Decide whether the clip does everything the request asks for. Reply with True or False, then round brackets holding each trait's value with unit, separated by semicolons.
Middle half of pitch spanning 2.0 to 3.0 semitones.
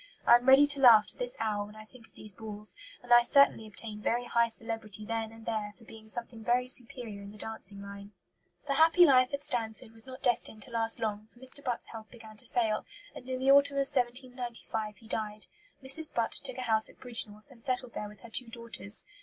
True (2.7 semitones)